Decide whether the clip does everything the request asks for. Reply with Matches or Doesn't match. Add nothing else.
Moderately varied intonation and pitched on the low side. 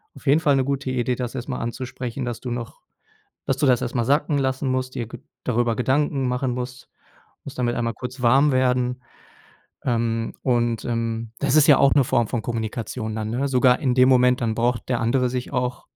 Doesn't match